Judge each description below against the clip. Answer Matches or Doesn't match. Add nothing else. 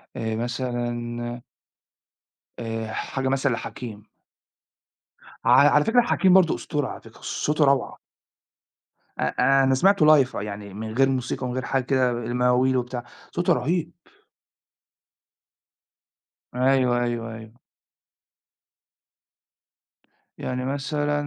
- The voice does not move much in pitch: Matches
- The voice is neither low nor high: Doesn't match